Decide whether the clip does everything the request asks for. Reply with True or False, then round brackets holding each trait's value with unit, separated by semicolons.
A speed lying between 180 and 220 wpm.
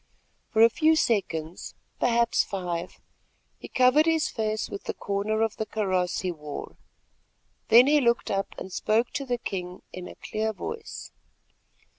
False (155 wpm)